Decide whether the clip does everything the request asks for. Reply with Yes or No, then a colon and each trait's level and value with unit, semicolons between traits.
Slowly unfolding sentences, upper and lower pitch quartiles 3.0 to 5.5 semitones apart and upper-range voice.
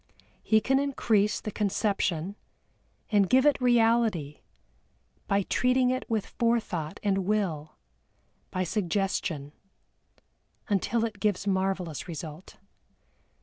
Yes: slow, 105 wpm; average, 4.1 semitones; high, 200 Hz